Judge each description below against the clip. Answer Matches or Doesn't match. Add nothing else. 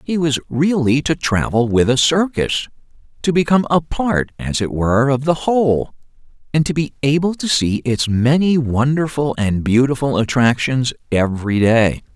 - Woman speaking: Doesn't match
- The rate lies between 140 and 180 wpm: Matches